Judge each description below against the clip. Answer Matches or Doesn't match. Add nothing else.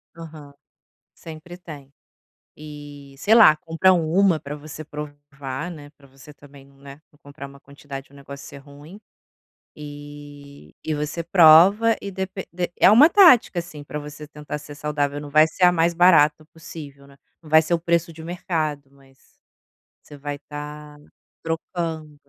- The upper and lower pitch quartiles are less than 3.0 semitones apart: Matches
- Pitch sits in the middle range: Matches